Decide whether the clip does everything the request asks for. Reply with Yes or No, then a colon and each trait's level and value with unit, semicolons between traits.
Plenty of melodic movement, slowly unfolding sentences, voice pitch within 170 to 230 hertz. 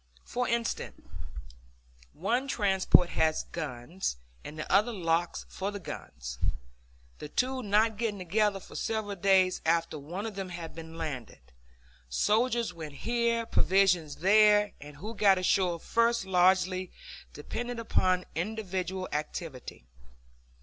No: average, 4.6 semitones; slow, 125 wpm; high, 190 Hz